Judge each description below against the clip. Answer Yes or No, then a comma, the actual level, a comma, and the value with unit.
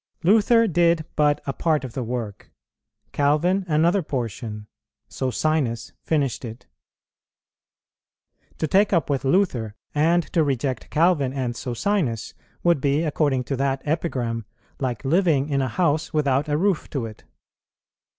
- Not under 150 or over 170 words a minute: No, slow, 135 wpm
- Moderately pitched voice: Yes, medium, 145 Hz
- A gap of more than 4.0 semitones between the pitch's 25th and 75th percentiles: Yes, average, 4.6 semitones